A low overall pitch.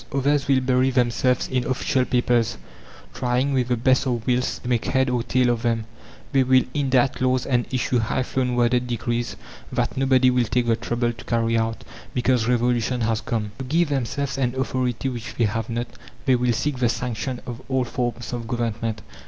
Yes: low, 125 Hz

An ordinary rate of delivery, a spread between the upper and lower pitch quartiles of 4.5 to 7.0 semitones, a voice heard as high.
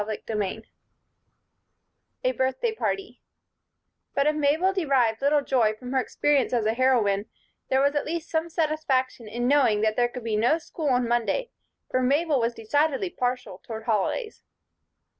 Yes: average, 160 wpm; average, 4.9 semitones; very high, 260 Hz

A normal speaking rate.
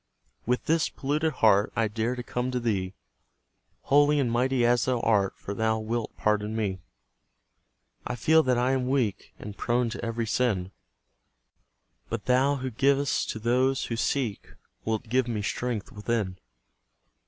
Yes: average, 155 wpm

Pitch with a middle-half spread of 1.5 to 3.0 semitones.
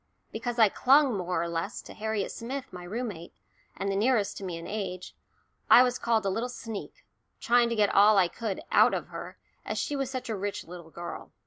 No: average, 4.6 semitones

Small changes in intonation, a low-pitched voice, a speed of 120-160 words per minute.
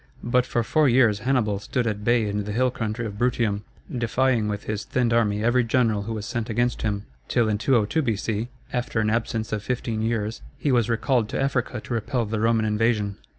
No: narrow, 2.3 semitones; low, 115 Hz; fast, 205 wpm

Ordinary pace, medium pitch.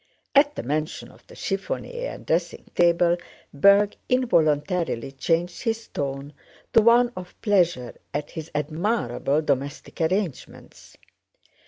No: slow, 120 wpm; medium, 170 Hz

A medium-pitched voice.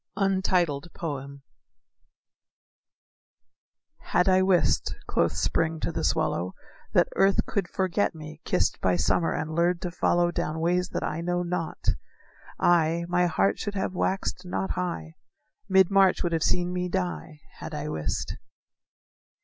Yes: medium, 175 Hz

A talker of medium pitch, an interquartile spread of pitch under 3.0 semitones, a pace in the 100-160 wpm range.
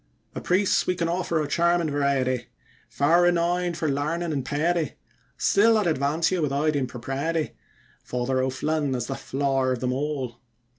No: medium, 150 Hz; average, 4.2 semitones; average, 155 wpm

